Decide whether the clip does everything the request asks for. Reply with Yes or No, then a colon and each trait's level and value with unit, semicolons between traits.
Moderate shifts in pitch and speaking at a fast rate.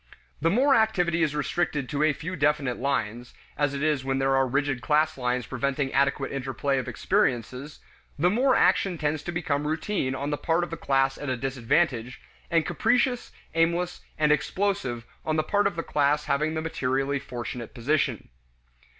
No: average, 3.7 semitones; average, 175 wpm